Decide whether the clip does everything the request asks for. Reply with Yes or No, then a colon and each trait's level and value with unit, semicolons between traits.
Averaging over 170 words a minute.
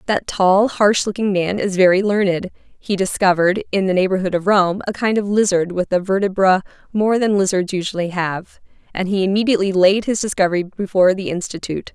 Yes: average, 180 wpm